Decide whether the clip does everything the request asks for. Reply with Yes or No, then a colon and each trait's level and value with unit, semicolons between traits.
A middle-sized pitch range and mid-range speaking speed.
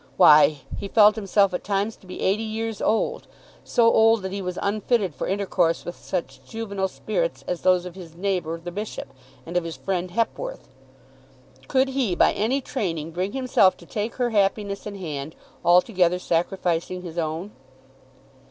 Yes: average, 3.7 semitones; average, 170 wpm